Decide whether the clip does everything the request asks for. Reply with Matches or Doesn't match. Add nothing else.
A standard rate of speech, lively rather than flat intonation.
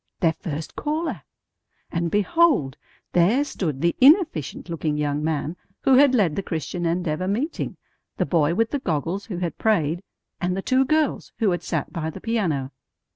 Matches